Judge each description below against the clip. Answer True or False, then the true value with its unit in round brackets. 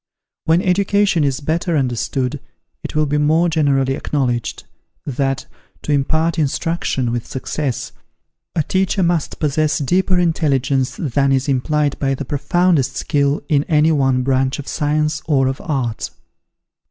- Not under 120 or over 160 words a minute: True (140 wpm)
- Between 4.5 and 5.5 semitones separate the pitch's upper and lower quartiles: False (3.2 semitones)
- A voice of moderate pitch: True (145 Hz)